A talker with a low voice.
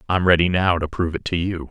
Yes: very low, 85 Hz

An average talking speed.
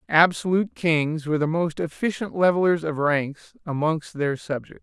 Yes: average, 150 wpm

